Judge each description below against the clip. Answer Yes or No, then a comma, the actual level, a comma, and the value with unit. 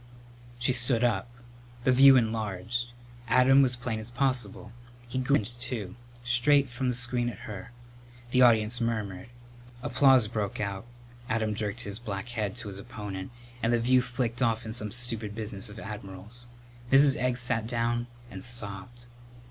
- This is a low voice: Yes, low, 120 Hz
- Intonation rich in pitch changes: No, average, 2.7 semitones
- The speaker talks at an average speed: Yes, average, 155 wpm